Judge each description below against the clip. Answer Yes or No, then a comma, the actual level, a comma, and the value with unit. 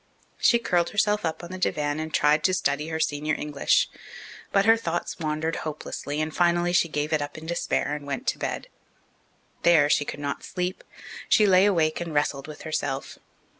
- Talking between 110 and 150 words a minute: No, average, 190 wpm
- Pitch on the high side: No, medium, 155 Hz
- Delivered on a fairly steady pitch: No, average, 3.0 semitones